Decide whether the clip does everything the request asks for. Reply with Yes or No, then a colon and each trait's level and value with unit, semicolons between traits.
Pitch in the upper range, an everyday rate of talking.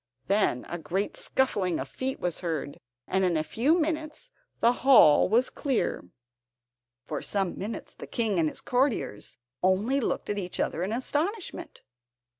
Yes: high, 205 Hz; average, 155 wpm